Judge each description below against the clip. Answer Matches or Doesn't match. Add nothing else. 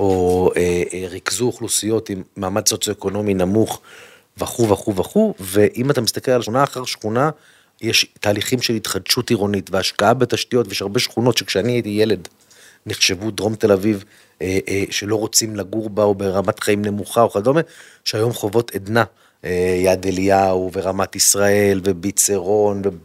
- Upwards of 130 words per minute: Matches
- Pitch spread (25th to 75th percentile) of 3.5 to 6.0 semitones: Doesn't match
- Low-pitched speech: Matches